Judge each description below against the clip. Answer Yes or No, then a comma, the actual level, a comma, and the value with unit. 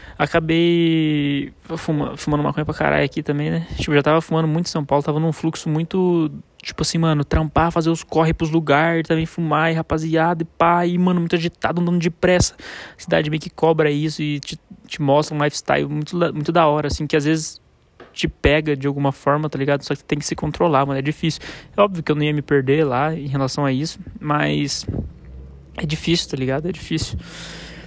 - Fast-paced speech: Yes, fast, 210 wpm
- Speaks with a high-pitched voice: No, medium, 155 Hz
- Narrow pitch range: Yes, narrow, 2.1 semitones